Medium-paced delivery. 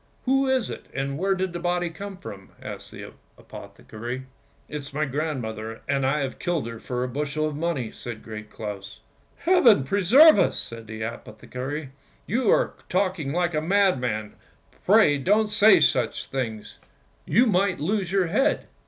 Yes: average, 185 wpm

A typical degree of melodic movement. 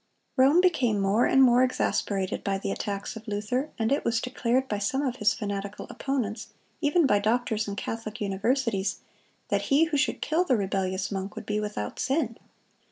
Yes: average, 4.6 semitones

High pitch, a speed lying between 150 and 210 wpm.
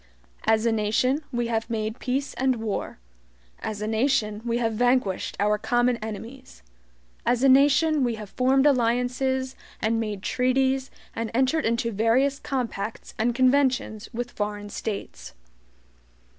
No: high, 240 Hz; average, 140 wpm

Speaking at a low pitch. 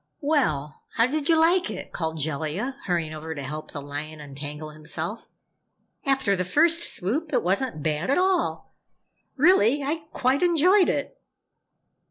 No: high, 200 Hz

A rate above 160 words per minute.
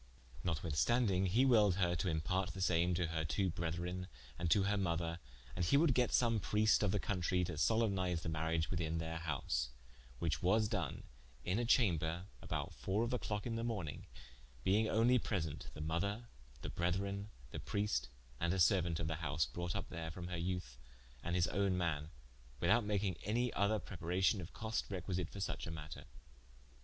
Yes: average, 185 wpm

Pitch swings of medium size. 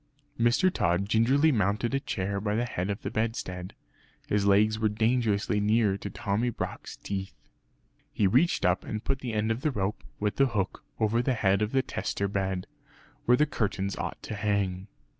Yes: average, 3.0 semitones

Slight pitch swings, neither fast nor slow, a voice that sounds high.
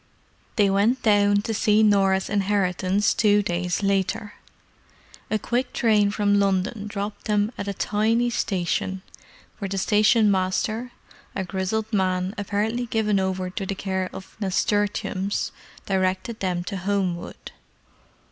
No: narrow, 1.9 semitones; slow, 130 wpm; high, 200 Hz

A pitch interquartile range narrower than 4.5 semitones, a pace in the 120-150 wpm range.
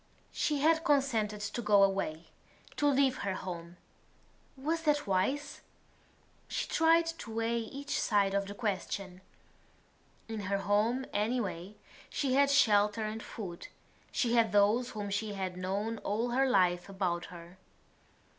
No: average, 5.1 semitones; average, 140 wpm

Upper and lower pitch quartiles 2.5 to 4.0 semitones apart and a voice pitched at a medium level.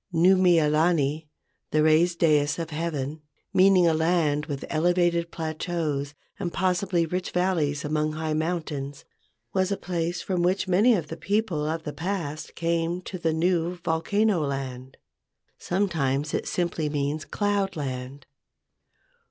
Yes: average, 3.0 semitones; medium, 165 Hz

